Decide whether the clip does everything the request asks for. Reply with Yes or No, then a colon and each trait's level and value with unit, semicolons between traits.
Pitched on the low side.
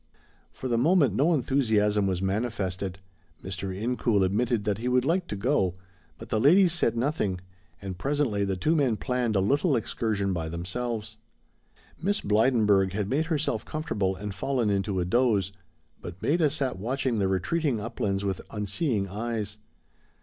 Yes: low, 110 Hz